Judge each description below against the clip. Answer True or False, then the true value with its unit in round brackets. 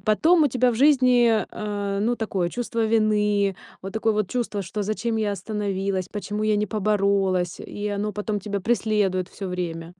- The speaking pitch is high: True (210 Hz)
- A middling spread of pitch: False (2.1 semitones)